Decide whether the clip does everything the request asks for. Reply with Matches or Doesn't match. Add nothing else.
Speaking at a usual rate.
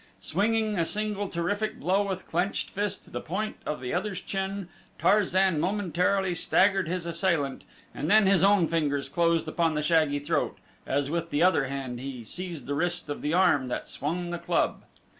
Matches